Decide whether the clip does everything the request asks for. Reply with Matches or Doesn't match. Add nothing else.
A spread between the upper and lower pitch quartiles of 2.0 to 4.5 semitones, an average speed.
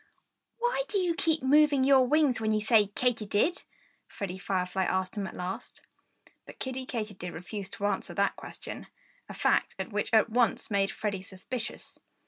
Doesn't match